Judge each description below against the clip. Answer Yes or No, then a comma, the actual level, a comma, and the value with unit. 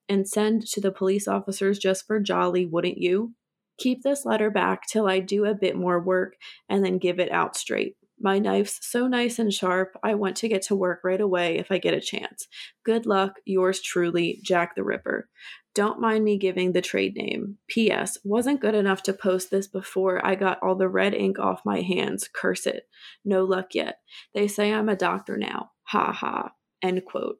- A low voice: No, high, 195 Hz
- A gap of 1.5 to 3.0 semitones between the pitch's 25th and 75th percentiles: Yes, narrow, 2.4 semitones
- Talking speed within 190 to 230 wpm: Yes, fast, 205 wpm